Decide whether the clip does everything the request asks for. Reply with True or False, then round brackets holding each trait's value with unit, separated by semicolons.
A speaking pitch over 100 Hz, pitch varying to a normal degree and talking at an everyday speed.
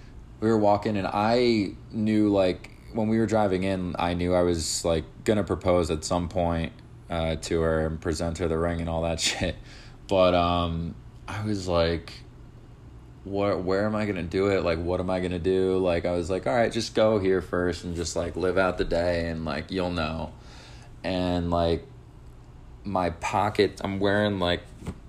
False (90 Hz; 3.1 semitones; 190 wpm)